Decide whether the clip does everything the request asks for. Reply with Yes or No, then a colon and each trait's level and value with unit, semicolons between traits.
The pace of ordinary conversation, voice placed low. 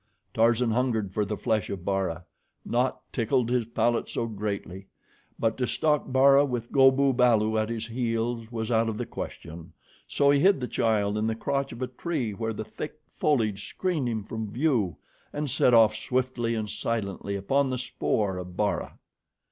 Yes: average, 180 wpm; low, 115 Hz